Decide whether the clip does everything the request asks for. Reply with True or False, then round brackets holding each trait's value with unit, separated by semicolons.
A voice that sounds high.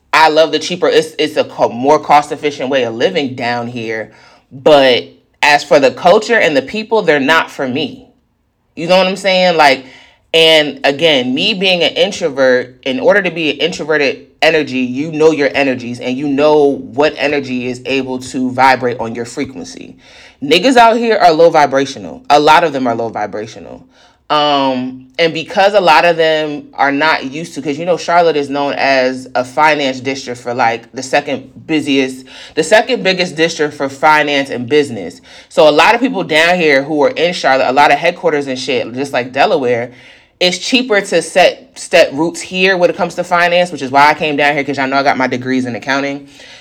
False (150 Hz)